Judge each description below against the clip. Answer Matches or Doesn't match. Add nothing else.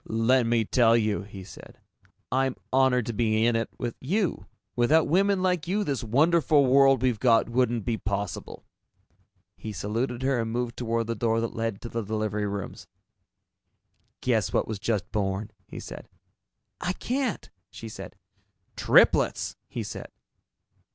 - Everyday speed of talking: Matches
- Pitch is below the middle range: Matches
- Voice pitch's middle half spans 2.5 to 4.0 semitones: Matches